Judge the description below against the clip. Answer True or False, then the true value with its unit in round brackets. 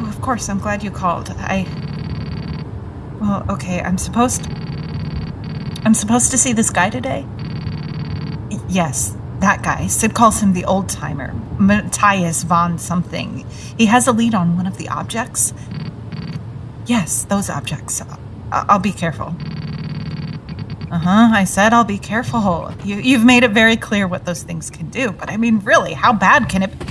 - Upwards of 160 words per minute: False (155 wpm)